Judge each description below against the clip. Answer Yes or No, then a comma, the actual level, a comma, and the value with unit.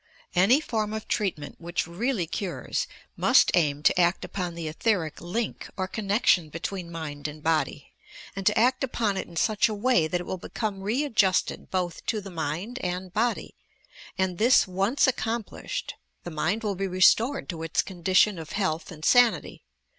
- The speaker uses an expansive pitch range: No, average, 4.3 semitones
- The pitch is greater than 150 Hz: Yes, high, 190 Hz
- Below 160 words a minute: No, average, 175 wpm